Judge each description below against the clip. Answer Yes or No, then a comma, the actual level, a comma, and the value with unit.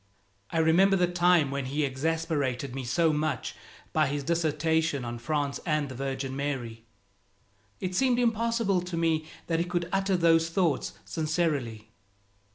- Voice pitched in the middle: Yes, medium, 160 Hz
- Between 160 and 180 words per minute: No, average, 150 wpm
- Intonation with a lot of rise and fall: No, average, 4.0 semitones